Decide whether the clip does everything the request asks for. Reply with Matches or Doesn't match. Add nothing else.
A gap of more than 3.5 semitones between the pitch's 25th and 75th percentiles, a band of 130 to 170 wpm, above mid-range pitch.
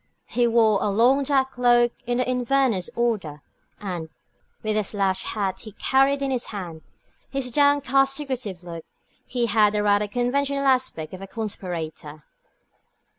Matches